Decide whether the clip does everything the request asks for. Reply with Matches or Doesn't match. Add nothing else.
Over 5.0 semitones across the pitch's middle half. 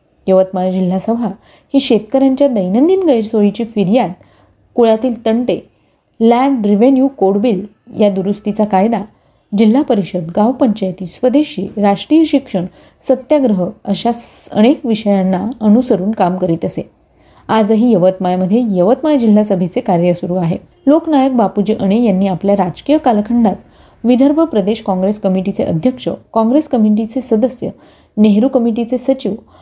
Doesn't match